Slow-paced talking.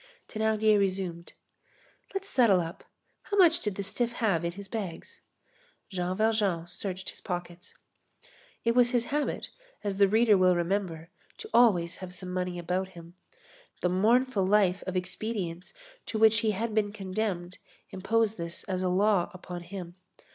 No: average, 155 wpm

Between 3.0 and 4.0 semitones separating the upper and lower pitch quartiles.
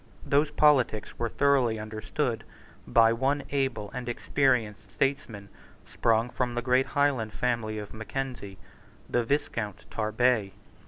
Yes: average, 3.7 semitones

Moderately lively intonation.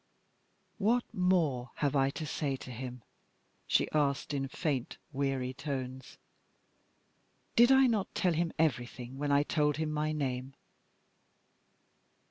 Yes: average, 3.2 semitones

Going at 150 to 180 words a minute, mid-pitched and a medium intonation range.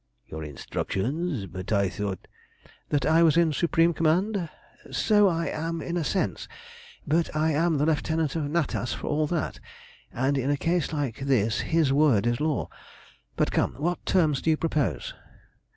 Yes: average, 170 wpm; medium, 155 Hz; average, 3.8 semitones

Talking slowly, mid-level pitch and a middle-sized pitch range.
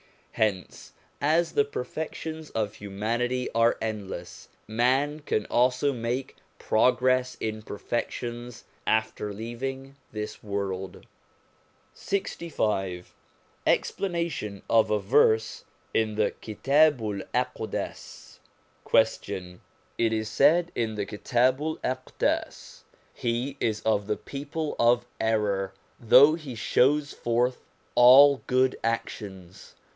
No: slow, 100 wpm; low, 120 Hz; average, 4.0 semitones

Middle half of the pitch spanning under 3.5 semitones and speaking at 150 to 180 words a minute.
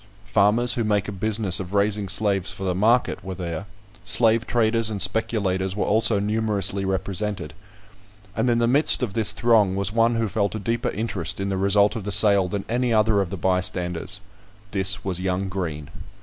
No: narrow, 2.6 semitones; average, 190 wpm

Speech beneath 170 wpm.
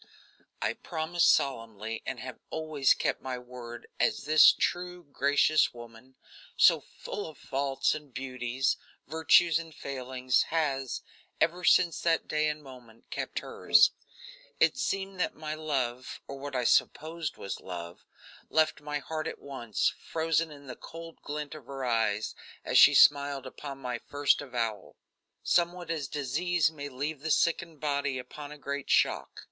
Yes: average, 150 wpm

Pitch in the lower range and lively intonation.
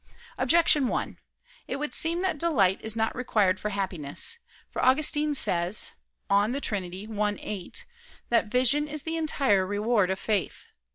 No: high, 225 Hz; wide, 6.8 semitones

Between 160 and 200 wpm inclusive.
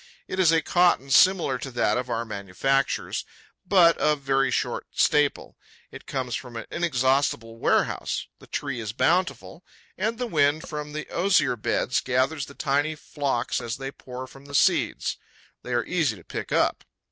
Yes: average, 170 wpm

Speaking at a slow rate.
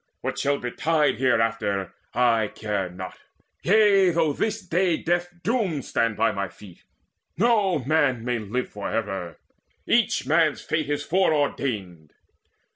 Yes: slow, 130 wpm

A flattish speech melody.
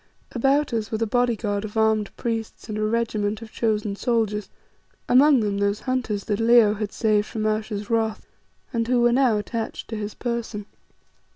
Yes: narrow, 2.0 semitones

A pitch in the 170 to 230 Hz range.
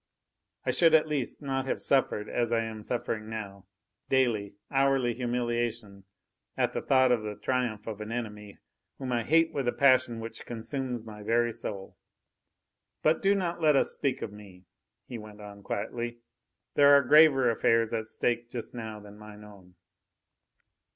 No: low, 120 Hz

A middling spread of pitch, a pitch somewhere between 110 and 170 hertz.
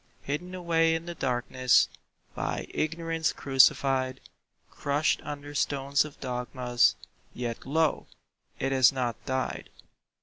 Yes: average, 3.6 semitones; medium, 140 Hz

